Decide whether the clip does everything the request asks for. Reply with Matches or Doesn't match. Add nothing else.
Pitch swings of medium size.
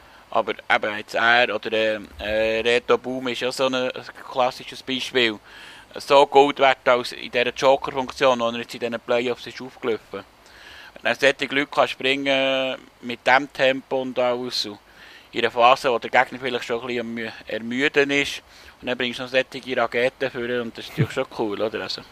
Doesn't match